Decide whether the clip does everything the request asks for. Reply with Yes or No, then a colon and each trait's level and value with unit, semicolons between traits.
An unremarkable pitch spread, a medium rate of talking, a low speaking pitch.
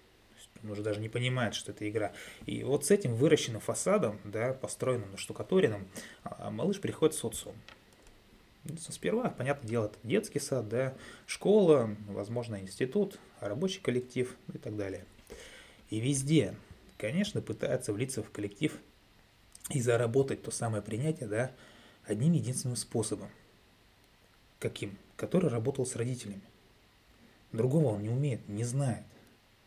Yes: average, 4.1 semitones; average, 125 wpm; low, 115 Hz